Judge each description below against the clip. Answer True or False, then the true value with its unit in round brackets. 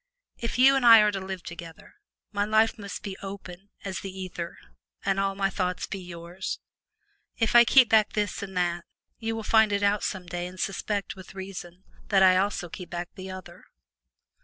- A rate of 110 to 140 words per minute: False (195 wpm)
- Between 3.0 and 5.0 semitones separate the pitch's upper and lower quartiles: False (2.4 semitones)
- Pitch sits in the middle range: False (195 Hz)